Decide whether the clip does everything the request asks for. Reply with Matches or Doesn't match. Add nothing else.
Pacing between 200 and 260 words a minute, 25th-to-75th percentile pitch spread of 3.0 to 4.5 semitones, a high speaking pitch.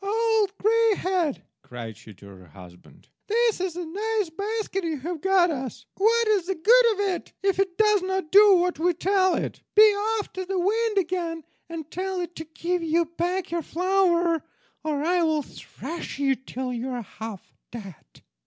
Doesn't match